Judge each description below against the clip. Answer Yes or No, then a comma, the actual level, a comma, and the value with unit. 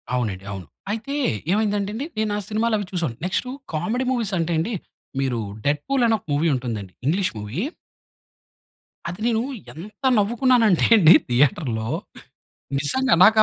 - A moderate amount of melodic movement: No, wide, 8.1 semitones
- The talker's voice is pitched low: No, medium, 185 Hz